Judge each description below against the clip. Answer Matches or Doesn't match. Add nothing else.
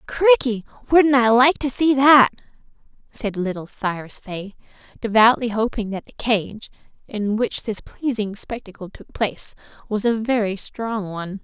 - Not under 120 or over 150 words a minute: Matches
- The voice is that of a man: Doesn't match